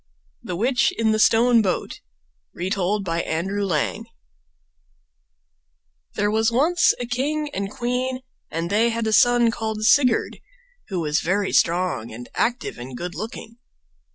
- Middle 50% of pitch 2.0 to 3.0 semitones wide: No, average, 5.0 semitones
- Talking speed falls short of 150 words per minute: Yes, average, 140 wpm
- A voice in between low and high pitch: No, high, 215 Hz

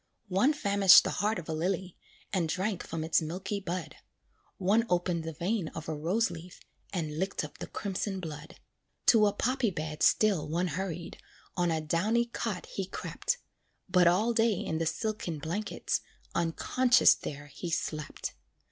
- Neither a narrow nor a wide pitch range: Yes, average, 4.2 semitones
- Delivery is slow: No, average, 165 wpm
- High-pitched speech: No, medium, 180 Hz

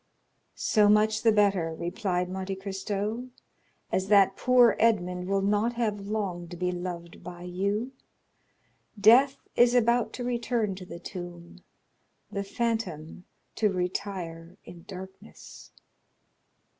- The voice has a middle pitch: No, high, 195 Hz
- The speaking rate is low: Yes, slow, 120 wpm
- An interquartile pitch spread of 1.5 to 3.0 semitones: No, average, 3.4 semitones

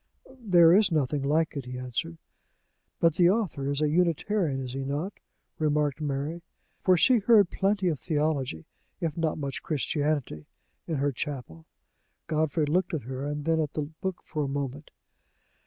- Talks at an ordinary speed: Yes, average, 160 wpm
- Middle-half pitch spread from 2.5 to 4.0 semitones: Yes, average, 3.6 semitones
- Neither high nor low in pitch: Yes, medium, 150 Hz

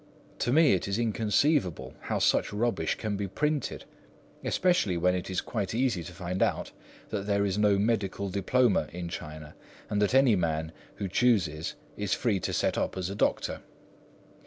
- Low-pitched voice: Yes, low, 100 Hz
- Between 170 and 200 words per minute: Yes, average, 175 wpm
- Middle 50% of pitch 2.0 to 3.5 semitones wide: No, average, 4.3 semitones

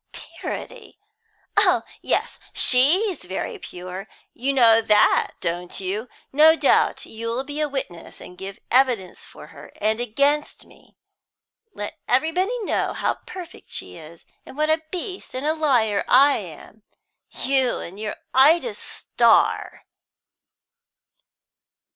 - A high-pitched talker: Yes, very high, 255 Hz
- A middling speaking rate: No, slow, 125 wpm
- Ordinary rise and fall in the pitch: No, wide, 6.8 semitones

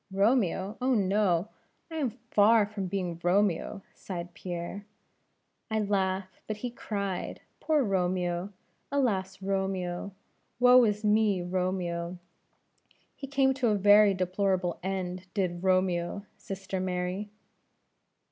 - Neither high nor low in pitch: No, high, 195 Hz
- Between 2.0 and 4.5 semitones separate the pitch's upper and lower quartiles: Yes, narrow, 2.5 semitones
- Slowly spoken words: Yes, slow, 120 wpm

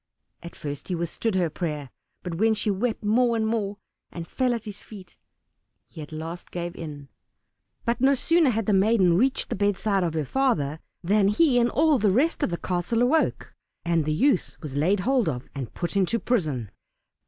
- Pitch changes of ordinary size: No, wide, 5.8 semitones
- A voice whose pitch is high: Yes, high, 195 Hz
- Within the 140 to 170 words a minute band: No, average, 195 wpm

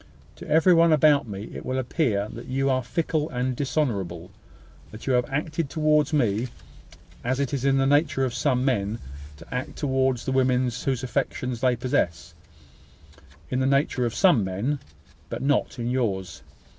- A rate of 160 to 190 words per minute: Yes, average, 170 wpm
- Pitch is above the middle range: No, low, 130 Hz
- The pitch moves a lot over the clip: No, average, 3.1 semitones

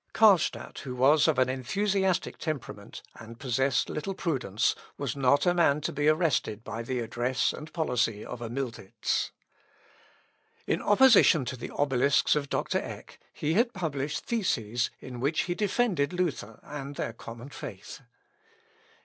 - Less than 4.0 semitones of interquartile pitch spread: No, average, 5.2 semitones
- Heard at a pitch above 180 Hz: No, medium, 140 Hz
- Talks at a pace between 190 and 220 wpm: No, average, 150 wpm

